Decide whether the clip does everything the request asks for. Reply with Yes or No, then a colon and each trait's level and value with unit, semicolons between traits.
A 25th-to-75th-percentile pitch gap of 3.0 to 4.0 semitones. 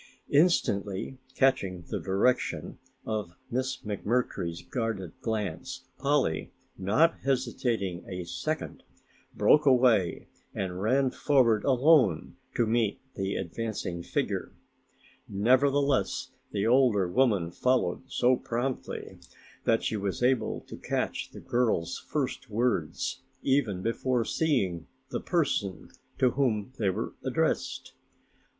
No: average, 5.1 semitones